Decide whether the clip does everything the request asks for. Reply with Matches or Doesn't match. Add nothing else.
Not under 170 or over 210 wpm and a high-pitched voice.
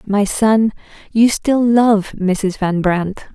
Doesn't match